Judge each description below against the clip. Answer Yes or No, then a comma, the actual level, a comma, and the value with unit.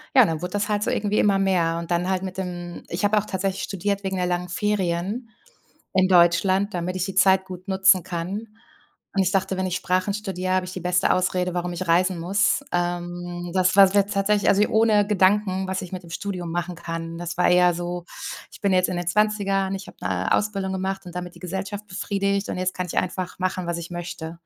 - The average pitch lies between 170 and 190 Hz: Yes, medium, 185 Hz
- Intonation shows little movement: Yes, narrow, 1.9 semitones